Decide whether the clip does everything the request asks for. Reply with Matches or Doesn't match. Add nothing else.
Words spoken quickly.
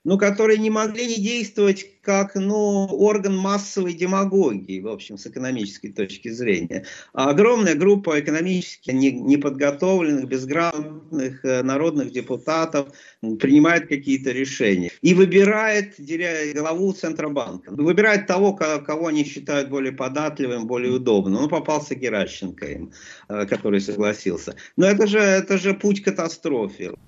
Doesn't match